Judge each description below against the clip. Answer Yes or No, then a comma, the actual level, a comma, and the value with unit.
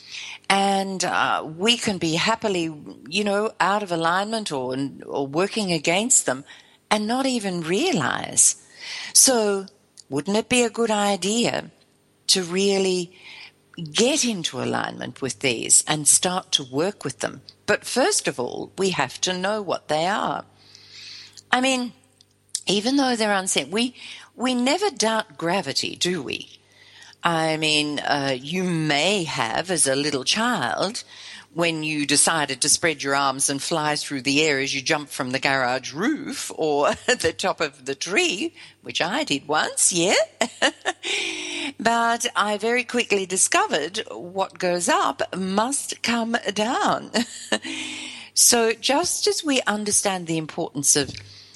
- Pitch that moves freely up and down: Yes, wide, 7.8 semitones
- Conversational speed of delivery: Yes, average, 145 wpm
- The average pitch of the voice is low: No, high, 190 Hz